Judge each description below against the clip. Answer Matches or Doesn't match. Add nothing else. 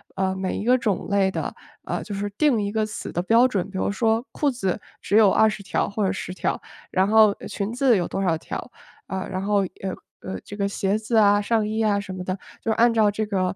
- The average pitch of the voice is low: Doesn't match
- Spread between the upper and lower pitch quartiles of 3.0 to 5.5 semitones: Doesn't match